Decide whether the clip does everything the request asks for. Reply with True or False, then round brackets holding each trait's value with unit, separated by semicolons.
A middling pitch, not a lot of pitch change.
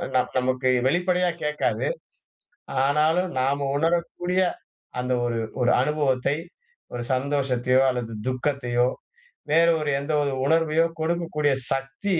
False (145 Hz; 4.2 semitones)